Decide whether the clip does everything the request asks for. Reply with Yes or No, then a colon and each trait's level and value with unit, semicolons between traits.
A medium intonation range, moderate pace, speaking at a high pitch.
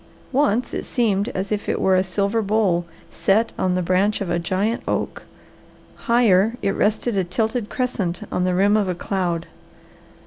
Yes: average, 3.2 semitones; average, 175 wpm; high, 200 Hz